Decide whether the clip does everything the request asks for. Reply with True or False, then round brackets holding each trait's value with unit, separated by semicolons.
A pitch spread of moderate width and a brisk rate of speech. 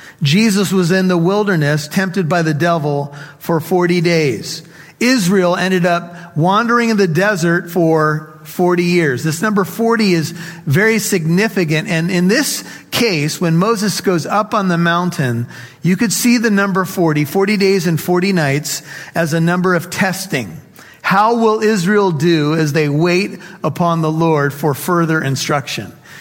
False (3.5 semitones; 155 wpm)